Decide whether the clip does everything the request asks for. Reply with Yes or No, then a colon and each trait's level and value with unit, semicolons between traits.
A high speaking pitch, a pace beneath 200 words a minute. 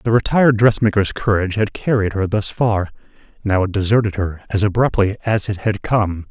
No: low, 105 Hz; average, 180 wpm